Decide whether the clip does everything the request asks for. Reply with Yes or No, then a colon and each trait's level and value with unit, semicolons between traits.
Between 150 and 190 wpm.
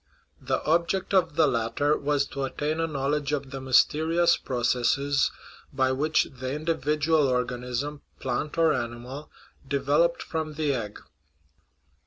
No: slow, 135 wpm